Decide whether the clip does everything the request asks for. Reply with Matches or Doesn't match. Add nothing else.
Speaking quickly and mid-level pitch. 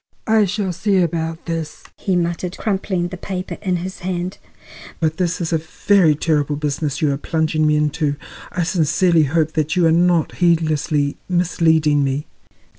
Doesn't match